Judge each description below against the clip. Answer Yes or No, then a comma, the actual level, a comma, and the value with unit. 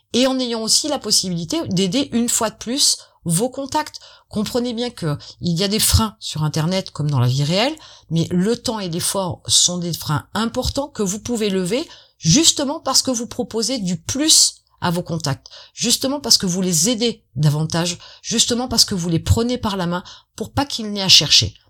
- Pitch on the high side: Yes, high, 210 Hz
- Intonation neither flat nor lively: No, wide, 6.3 semitones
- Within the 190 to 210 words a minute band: Yes, average, 200 wpm